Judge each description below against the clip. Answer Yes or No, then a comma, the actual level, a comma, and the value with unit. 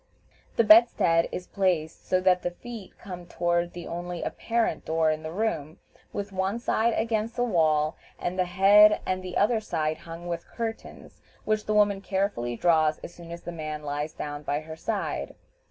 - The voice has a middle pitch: Yes, medium, 175 Hz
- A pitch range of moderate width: Yes, average, 4.7 semitones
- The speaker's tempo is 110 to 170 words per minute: No, average, 180 wpm